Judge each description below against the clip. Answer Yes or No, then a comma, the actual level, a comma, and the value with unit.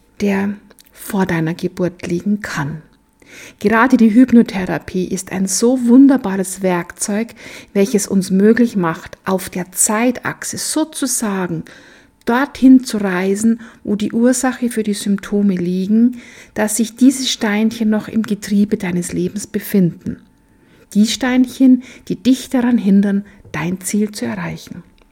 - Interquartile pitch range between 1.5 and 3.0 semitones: No, average, 4.0 semitones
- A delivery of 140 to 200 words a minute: No, slow, 125 wpm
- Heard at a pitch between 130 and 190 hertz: No, high, 210 Hz